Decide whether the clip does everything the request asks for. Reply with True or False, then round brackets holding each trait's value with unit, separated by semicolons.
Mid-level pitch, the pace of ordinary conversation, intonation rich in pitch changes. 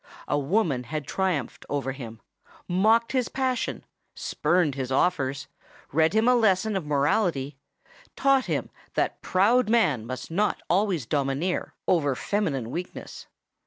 False (170 Hz; 115 wpm; 7.6 semitones)